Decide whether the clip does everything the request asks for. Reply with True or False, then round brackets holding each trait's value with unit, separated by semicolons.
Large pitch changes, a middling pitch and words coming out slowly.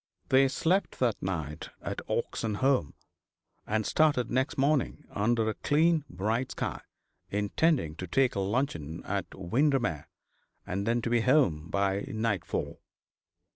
False (5.8 semitones; 115 Hz; 125 wpm)